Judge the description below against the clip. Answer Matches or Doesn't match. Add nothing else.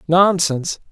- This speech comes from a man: Matches